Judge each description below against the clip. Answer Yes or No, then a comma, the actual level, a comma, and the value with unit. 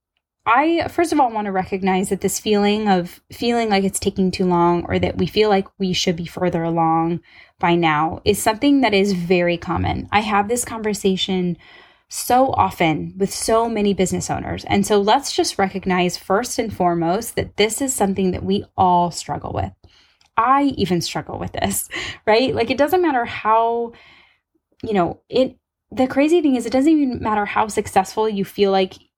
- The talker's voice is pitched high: Yes, high, 200 Hz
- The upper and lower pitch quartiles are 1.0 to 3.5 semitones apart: No, average, 4.3 semitones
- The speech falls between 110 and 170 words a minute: No, average, 185 wpm